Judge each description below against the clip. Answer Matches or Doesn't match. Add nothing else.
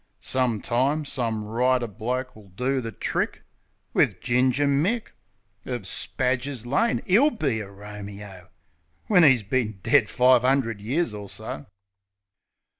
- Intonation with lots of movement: Doesn't match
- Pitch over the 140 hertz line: Doesn't match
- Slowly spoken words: Matches